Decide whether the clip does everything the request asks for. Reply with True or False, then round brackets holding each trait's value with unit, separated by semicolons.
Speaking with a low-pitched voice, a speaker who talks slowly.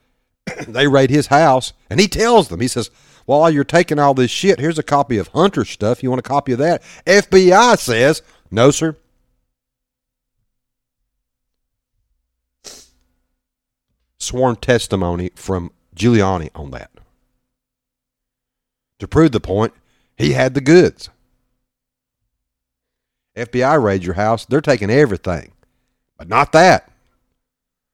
True (125 Hz; 120 wpm)